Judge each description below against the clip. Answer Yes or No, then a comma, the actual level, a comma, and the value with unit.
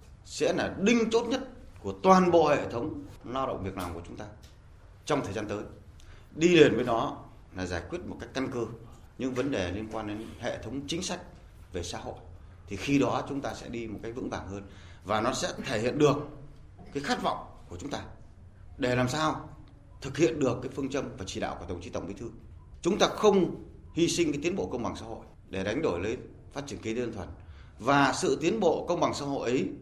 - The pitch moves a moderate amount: No, wide, 7.0 semitones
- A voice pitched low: Yes, low, 115 Hz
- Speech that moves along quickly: No, average, 235 wpm